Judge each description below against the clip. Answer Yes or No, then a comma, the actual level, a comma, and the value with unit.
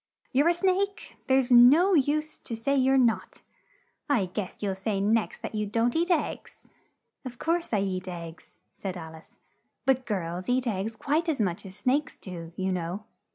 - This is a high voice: Yes, high, 230 Hz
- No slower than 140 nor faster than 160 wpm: No, average, 185 wpm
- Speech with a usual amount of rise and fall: No, wide, 6.8 semitones